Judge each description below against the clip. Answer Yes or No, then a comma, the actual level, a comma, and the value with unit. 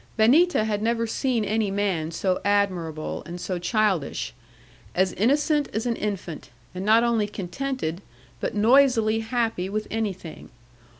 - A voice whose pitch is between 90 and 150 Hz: No, high, 215 Hz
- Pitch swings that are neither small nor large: Yes, average, 3.7 semitones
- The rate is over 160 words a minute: No, slow, 135 wpm